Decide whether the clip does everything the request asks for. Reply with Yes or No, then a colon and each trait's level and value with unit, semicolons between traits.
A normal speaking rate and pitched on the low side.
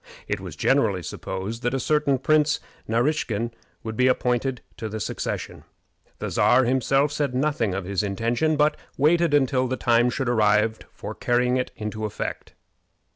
Yes: average, 160 wpm; low, 125 Hz